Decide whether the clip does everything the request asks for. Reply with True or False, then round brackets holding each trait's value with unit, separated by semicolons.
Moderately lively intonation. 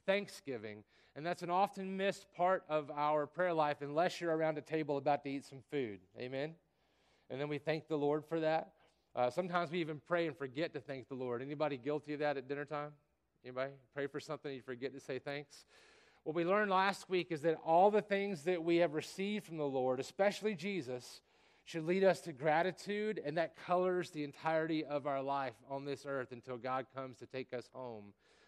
True (4.1 semitones)